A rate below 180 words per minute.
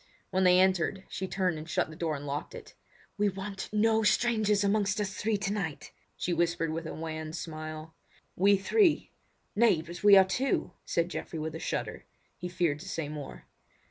No: average, 185 wpm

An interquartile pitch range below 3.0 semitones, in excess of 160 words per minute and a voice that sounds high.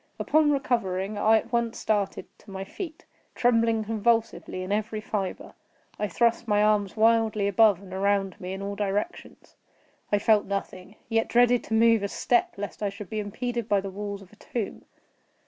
Yes: narrow, 2.5 semitones; average, 180 wpm; high, 210 Hz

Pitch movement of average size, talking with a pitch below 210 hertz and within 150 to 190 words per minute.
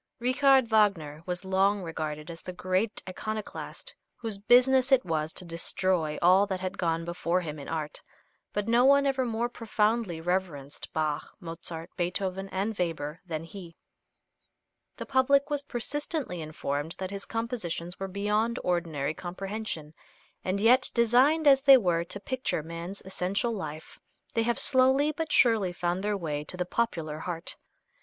No: wide, 5.8 semitones; high, 190 Hz; average, 155 wpm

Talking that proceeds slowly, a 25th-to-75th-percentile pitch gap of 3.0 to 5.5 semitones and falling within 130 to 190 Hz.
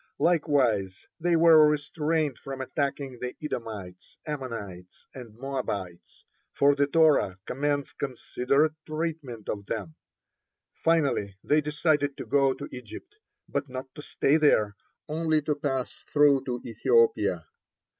Yes: slow, 125 wpm; average, 3.8 semitones; medium, 140 Hz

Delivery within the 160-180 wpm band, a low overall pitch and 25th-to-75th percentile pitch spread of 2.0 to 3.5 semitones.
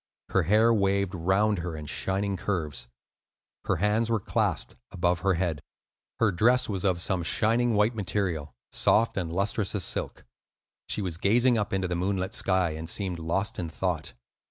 Yes: average, 170 wpm; very low, 95 Hz; average, 3.2 semitones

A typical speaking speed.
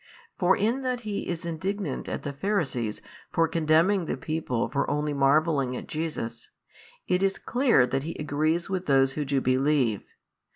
Yes: average, 165 wpm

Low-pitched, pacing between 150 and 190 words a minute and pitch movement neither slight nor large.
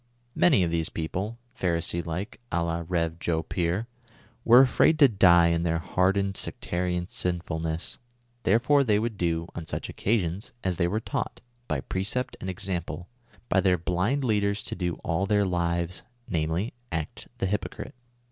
Yes: very low, 90 Hz; average, 165 wpm; average, 3.4 semitones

